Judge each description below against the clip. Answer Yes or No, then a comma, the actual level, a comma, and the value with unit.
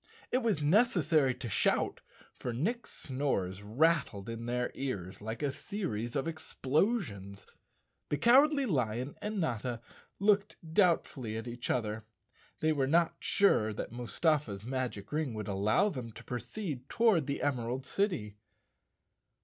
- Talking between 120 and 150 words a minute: Yes, average, 140 wpm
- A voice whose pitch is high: No, low, 135 Hz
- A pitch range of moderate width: No, wide, 6.8 semitones